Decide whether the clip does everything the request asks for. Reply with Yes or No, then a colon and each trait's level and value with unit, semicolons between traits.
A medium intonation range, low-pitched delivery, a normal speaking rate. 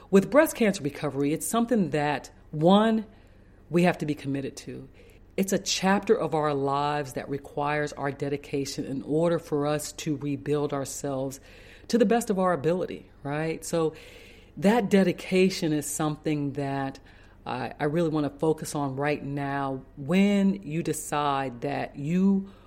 No: average, 3.7 semitones; medium, 150 Hz; average, 150 wpm